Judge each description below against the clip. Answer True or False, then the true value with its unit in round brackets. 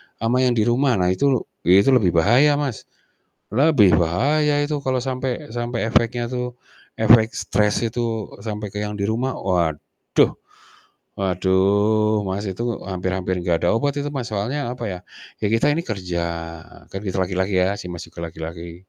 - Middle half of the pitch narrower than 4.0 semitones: False (4.9 semitones)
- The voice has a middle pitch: False (110 Hz)